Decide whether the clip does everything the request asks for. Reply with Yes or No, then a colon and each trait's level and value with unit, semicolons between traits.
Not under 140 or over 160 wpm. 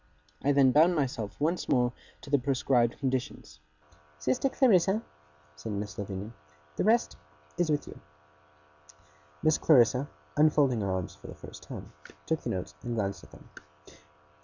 Yes: average, 150 wpm